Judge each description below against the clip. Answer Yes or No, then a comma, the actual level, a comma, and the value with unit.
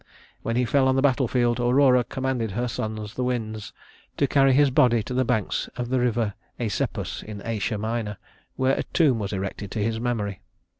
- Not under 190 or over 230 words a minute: Yes, average, 195 wpm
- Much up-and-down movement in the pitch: No, average, 3.0 semitones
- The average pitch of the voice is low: Yes, low, 120 Hz